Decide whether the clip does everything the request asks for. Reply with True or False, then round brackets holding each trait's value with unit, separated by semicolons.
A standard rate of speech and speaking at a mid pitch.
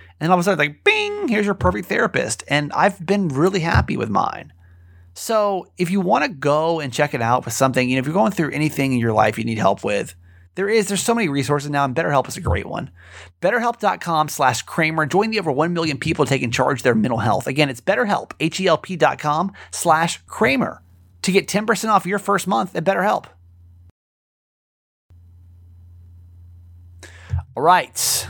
True (190 wpm; 145 Hz)